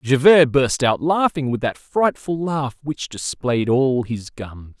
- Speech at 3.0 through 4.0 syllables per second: Yes, 3.7 syllables/s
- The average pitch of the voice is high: No, low, 135 Hz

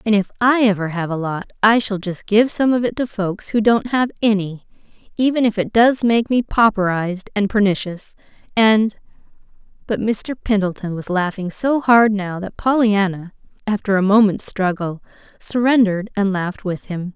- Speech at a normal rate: Yes, average, 170 wpm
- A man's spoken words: No, female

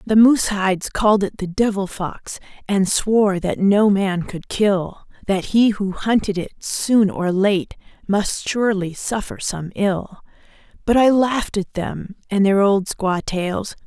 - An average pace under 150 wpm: No, average, 170 wpm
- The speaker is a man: No, female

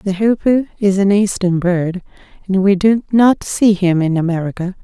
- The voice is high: Yes, high, 195 Hz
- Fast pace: No, average, 175 wpm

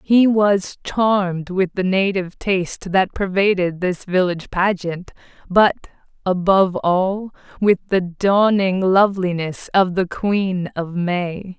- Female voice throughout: Yes, female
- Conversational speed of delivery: No, slow, 125 wpm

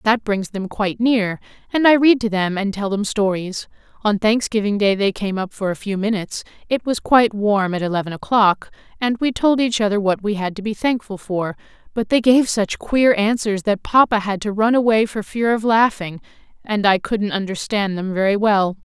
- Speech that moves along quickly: Yes, fast, 210 wpm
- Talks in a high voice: Yes, high, 210 Hz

